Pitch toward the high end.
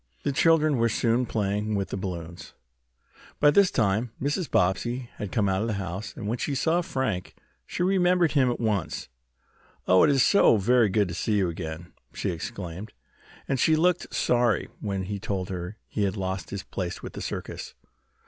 No: low, 105 Hz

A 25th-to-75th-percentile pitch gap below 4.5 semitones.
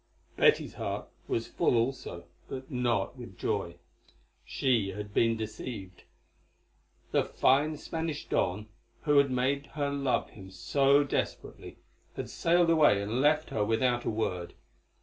No: average, 5.2 semitones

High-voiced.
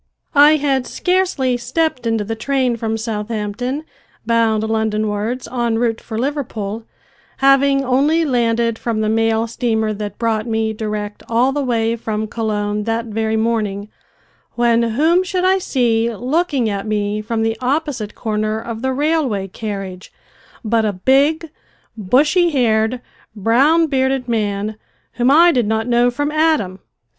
Yes: high, 230 Hz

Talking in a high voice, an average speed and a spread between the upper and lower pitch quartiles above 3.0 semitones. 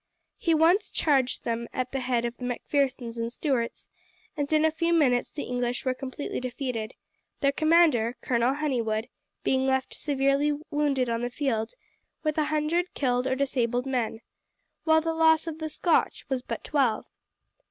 Yes: very high, 265 Hz; average, 170 wpm; average, 3.7 semitones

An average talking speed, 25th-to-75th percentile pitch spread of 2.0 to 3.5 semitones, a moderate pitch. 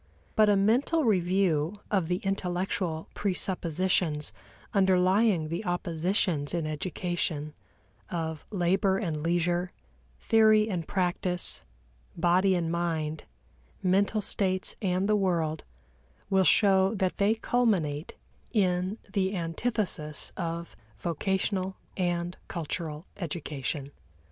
No: slow, 100 wpm; average, 2.9 semitones; medium, 180 Hz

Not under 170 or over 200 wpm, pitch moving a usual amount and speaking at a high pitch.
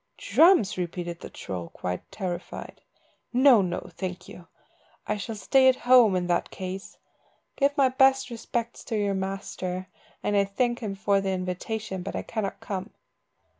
No: average, 160 wpm; average, 4.4 semitones; high, 200 Hz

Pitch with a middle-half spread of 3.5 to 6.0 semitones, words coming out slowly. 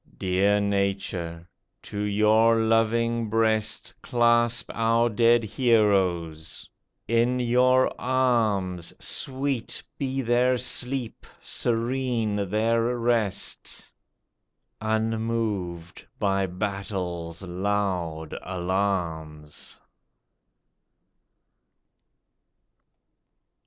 Yes: average, 3.8 semitones; slow, 65 wpm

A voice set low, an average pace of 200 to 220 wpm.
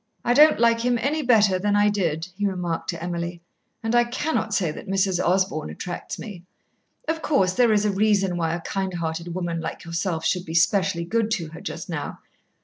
No: high, 190 Hz; fast, 205 wpm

